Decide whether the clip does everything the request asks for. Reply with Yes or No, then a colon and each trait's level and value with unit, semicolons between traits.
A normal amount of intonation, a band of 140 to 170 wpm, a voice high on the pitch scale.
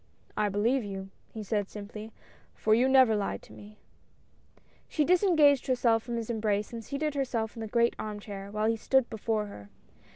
No: average, 3.3 semitones; average, 190 wpm; high, 225 Hz